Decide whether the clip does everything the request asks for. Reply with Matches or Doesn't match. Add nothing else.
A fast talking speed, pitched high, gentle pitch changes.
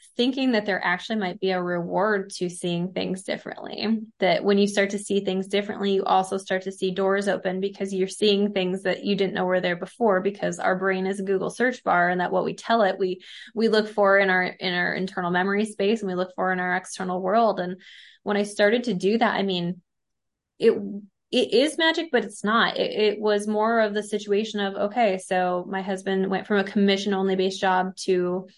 Matches